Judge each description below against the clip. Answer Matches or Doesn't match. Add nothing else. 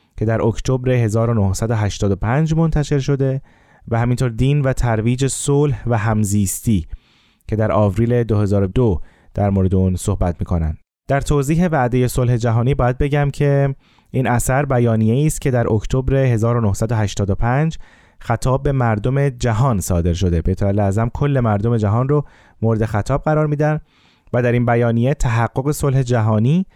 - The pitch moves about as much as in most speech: Matches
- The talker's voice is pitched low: Matches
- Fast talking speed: Doesn't match